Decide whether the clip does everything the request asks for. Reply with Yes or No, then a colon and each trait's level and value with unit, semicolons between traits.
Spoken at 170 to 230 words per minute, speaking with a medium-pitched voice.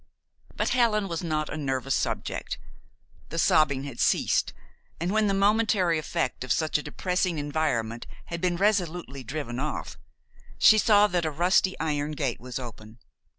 No: average, 155 wpm; medium, 155 Hz